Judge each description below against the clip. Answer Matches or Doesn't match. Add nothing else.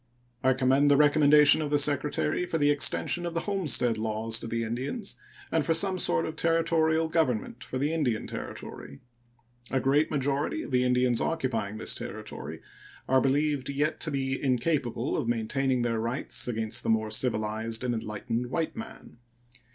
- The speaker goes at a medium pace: Matches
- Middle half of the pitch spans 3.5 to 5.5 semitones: Matches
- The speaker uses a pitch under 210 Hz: Matches